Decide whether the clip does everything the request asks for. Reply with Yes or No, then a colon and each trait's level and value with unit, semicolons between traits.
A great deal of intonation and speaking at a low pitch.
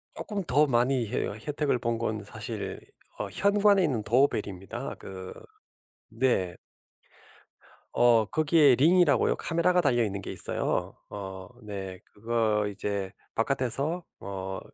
Yes: wide, 6.4 semitones; low, 120 Hz